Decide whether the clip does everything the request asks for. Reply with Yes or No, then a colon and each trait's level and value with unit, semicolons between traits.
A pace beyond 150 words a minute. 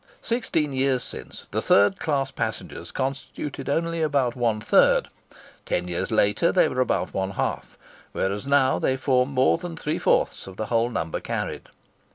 Yes: average, 165 wpm